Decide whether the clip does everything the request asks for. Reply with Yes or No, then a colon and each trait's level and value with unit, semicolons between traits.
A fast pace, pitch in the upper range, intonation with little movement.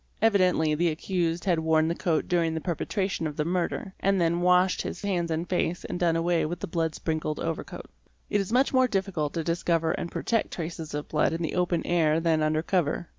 No: fast, 220 wpm; medium, 170 Hz; narrow, 2.1 semitones